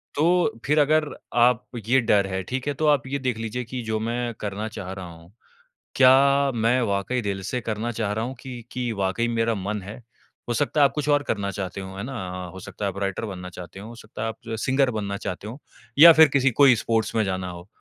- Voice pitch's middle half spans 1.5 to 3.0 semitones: No, average, 4.7 semitones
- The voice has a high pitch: No, low, 115 Hz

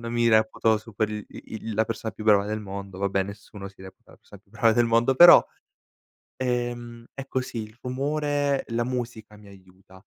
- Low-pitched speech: Yes, low, 110 Hz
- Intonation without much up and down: No, average, 3.0 semitones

